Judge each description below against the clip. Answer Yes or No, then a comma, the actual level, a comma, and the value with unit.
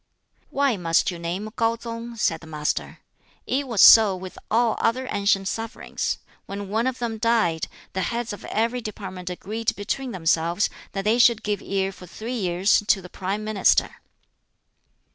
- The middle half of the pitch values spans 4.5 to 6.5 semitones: No, average, 3.7 semitones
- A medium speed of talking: Yes, average, 165 wpm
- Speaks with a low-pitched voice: No, high, 210 Hz